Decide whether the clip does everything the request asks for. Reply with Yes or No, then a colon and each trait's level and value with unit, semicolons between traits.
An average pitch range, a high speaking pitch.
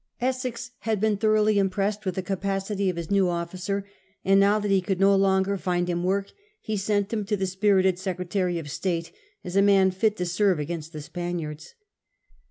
No: narrow, 2.2 semitones; high, 195 Hz